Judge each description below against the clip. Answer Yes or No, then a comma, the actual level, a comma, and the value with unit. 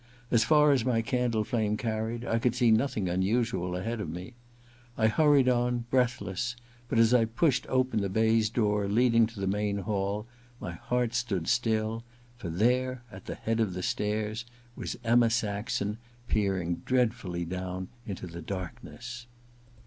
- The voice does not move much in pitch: No, average, 3.3 semitones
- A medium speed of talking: Yes, average, 160 wpm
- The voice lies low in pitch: Yes, low, 110 Hz